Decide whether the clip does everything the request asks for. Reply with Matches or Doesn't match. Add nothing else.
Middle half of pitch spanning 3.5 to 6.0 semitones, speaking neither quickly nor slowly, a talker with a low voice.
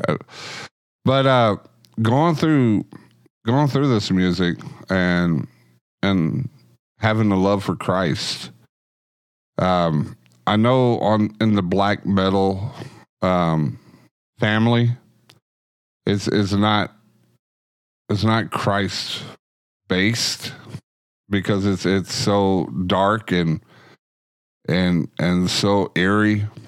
Doesn't match